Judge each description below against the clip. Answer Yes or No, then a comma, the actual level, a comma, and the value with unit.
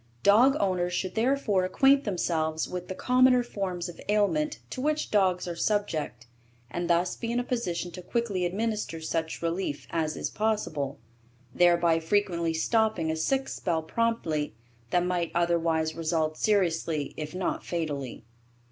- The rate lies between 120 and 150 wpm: Yes, average, 145 wpm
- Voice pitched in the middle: Yes, medium, 180 Hz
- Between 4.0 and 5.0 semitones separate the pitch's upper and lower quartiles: Yes, average, 4.7 semitones